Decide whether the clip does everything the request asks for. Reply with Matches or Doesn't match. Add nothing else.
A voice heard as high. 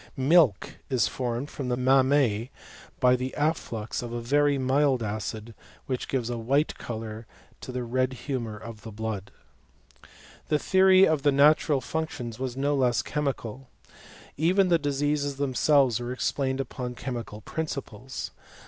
Doesn't match